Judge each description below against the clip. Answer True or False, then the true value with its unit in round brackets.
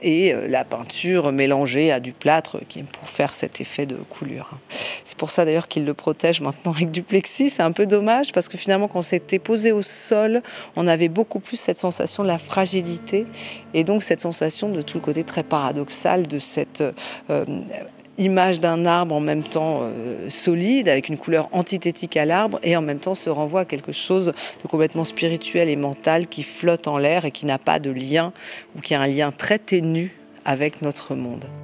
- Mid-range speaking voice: True (170 Hz)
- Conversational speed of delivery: True (205 wpm)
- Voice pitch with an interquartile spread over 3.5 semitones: True (3.9 semitones)